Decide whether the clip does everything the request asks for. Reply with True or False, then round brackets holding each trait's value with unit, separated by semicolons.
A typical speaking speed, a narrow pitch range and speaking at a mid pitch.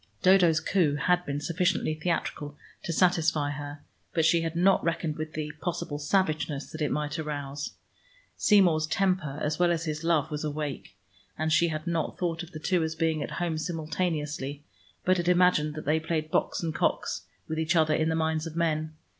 True (190 wpm; 2.0 semitones; 160 Hz)